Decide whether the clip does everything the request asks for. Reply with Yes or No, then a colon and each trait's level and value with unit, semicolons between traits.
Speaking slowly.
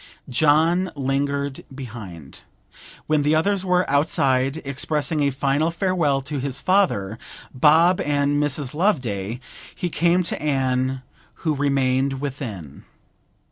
Yes: slow, 115 wpm